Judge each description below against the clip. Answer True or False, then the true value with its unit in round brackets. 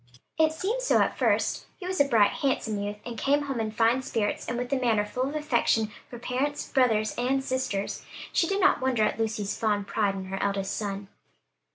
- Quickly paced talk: True (210 wpm)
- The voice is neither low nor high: False (240 Hz)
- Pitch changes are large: False (4.6 semitones)